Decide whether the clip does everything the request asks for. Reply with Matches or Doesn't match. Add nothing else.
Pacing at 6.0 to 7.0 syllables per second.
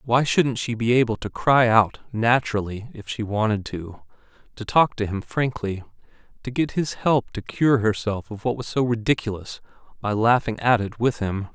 Doesn't match